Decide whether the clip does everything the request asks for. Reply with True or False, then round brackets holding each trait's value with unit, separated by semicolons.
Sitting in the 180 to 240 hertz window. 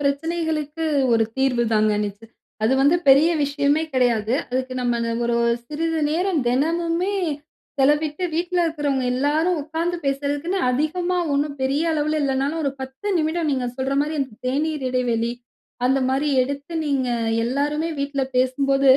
False (280 Hz)